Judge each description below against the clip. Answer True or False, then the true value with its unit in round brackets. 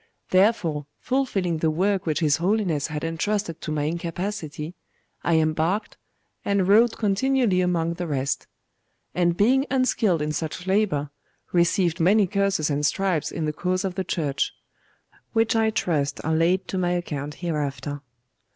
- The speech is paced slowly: False (150 wpm)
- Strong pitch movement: False (4.2 semitones)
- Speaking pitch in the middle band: True (175 Hz)